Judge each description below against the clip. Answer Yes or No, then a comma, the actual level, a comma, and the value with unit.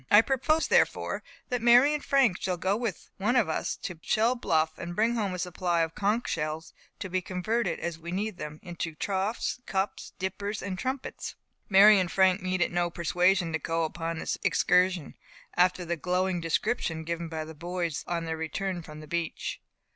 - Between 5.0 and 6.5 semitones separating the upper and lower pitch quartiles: No, average, 3.6 semitones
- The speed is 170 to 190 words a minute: Yes, average, 185 wpm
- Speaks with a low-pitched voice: No, medium, 180 Hz